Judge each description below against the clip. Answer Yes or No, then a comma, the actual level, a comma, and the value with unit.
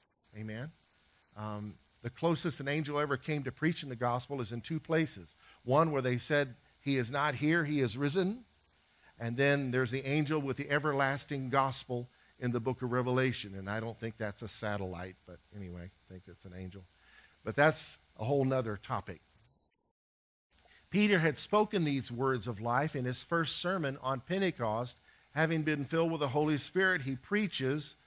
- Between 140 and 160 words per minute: No, average, 175 wpm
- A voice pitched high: No, low, 130 Hz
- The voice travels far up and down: Yes, wide, 5.8 semitones